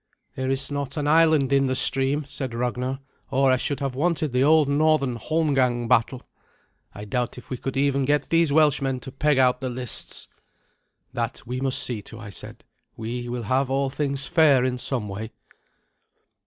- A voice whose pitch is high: No, low, 135 Hz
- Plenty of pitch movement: No, narrow, 2.4 semitones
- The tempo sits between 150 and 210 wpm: Yes, average, 180 wpm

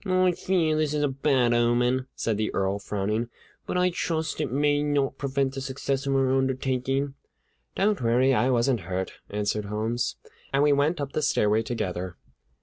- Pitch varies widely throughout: No, average, 4.0 semitones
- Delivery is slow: No, average, 180 wpm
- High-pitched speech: No, low, 135 Hz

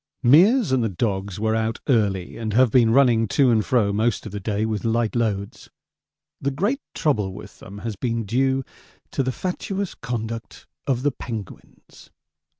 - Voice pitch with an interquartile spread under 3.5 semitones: No, average, 3.8 semitones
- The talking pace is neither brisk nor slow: Yes, average, 170 wpm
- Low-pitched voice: Yes, low, 115 Hz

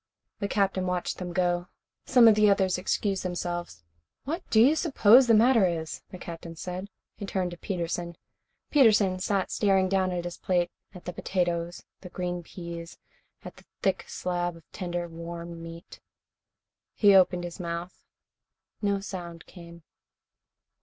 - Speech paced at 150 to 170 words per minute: Yes, average, 155 wpm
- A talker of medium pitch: Yes, medium, 180 Hz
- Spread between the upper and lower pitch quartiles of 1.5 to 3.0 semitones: Yes, narrow, 2.4 semitones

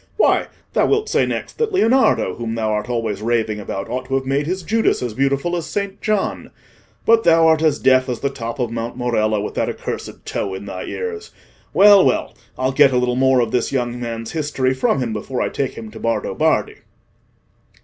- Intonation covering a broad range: Yes, wide, 5.8 semitones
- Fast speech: Yes, fast, 210 wpm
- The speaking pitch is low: Yes, low, 130 Hz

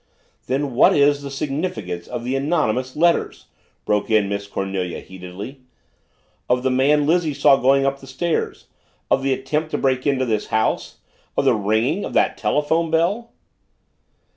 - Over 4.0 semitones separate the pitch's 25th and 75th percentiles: Yes, average, 5.2 semitones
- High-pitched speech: No, low, 135 Hz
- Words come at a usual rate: Yes, average, 160 wpm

